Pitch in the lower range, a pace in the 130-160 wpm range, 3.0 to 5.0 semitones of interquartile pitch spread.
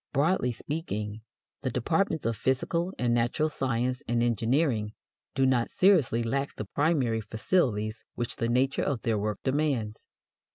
Yes: low, 125 Hz; average, 140 wpm; average, 4.1 semitones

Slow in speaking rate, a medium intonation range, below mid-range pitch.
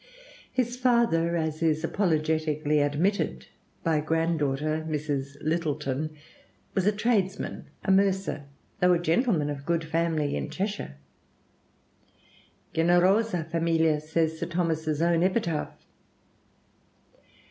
No: slow, 110 wpm; average, 3.0 semitones; medium, 165 Hz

